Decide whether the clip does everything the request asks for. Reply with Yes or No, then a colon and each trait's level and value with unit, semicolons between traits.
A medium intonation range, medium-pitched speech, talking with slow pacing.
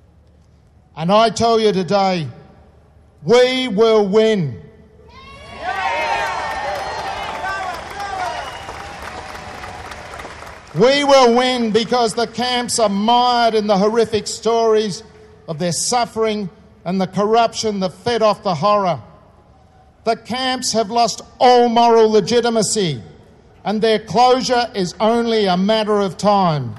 No: average, 4.0 semitones; high, 220 Hz; slow, 105 wpm